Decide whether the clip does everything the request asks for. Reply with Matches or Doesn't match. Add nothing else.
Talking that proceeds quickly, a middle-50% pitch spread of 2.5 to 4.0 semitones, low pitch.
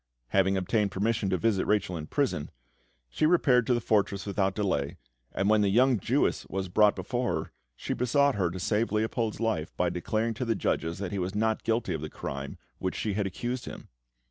Matches